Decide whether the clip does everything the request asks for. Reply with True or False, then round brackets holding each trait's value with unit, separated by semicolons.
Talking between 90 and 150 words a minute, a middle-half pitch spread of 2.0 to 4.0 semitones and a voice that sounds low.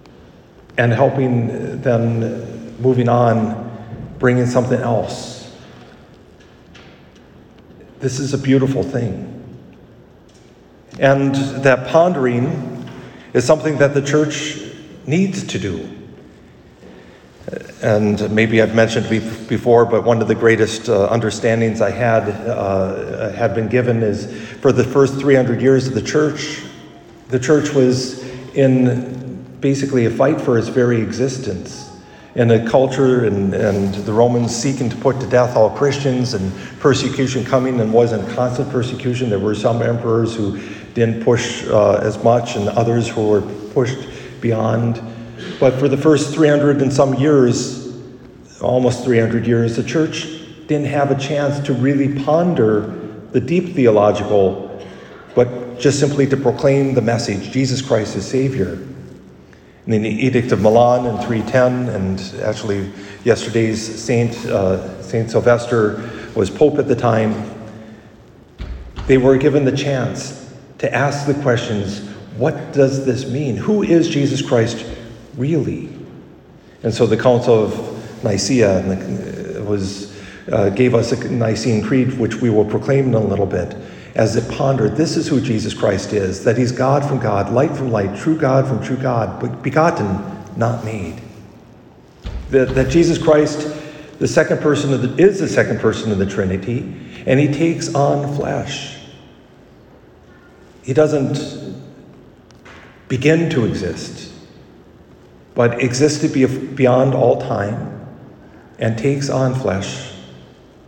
True (135 wpm; 3.6 semitones; 125 Hz)